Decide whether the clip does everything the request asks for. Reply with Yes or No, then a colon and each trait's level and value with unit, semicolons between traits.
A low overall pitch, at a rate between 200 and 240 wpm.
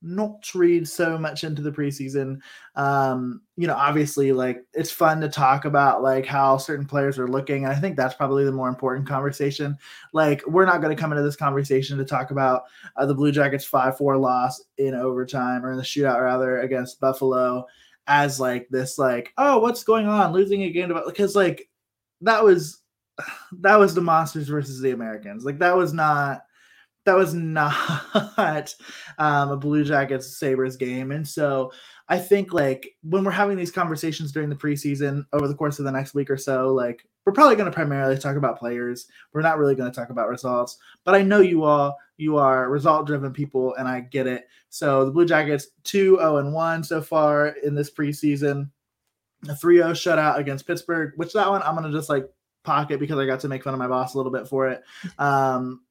No: medium, 145 Hz; fast, 205 wpm